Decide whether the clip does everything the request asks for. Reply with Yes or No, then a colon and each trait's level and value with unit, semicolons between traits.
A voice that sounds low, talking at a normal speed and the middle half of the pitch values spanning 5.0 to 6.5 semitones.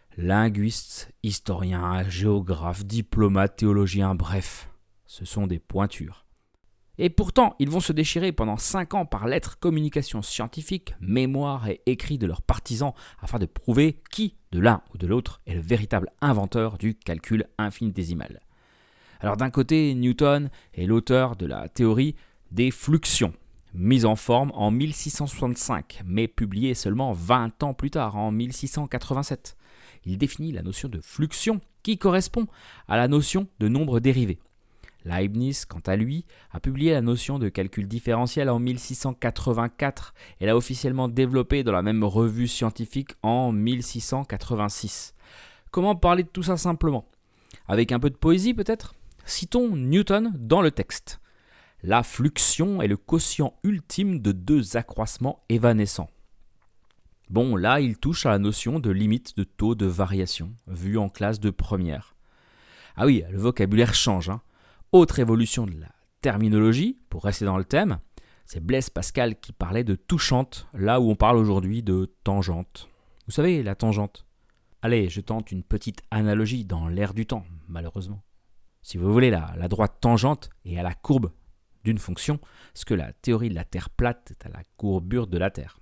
Yes: low, 110 Hz; average, 160 wpm; wide, 5.4 semitones